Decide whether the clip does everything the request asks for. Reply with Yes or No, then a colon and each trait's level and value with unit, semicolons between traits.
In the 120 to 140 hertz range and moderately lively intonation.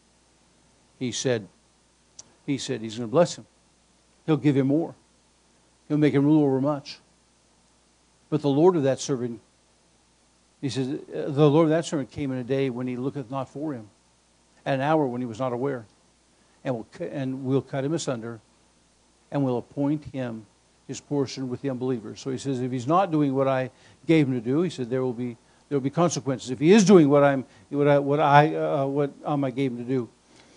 Yes: low, 135 Hz; average, 3.2 semitones